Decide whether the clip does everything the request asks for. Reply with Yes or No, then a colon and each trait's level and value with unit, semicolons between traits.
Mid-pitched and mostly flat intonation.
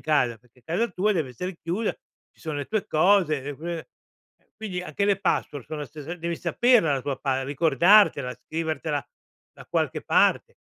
No: medium, 160 Hz; average, 4.4 semitones